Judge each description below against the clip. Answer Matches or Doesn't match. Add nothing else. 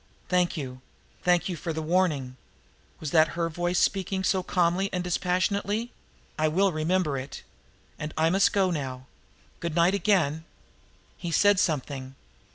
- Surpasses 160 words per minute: Doesn't match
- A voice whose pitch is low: Doesn't match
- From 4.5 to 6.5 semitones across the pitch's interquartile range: Doesn't match